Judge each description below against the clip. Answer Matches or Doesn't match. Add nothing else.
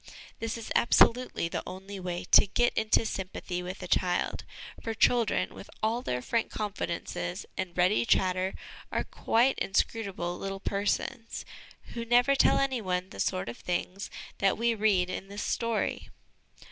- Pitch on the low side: Doesn't match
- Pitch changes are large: Doesn't match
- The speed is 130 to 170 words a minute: Matches